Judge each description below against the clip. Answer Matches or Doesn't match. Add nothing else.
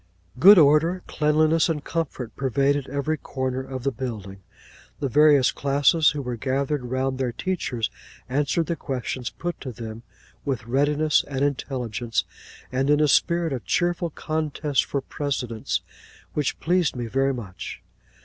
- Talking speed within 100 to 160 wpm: Matches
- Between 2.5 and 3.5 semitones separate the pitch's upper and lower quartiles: Matches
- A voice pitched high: Doesn't match